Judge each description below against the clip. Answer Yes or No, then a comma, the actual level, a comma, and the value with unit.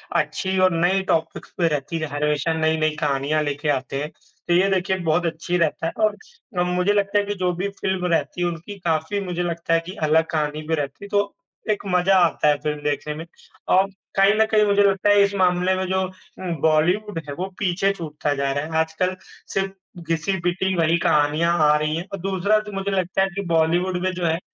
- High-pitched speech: No, medium, 175 Hz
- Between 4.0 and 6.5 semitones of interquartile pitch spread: No, average, 3.4 semitones